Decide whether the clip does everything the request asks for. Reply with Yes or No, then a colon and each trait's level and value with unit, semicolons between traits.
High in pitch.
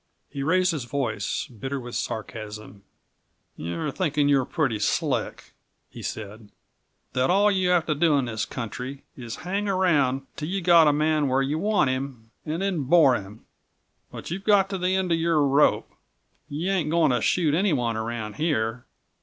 No: medium, 145 Hz